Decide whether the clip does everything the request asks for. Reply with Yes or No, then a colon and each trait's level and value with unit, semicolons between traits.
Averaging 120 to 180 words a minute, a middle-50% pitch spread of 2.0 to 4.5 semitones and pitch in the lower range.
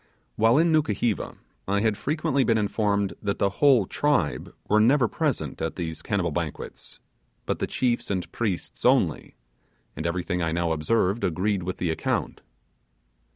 No: average, 155 wpm; average, 5.2 semitones; low, 100 Hz